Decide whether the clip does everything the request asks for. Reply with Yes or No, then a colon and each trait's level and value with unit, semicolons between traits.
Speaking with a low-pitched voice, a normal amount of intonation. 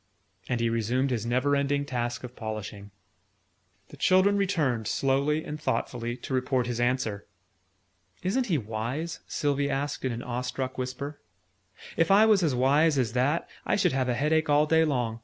Yes: low, 130 Hz; average, 3.9 semitones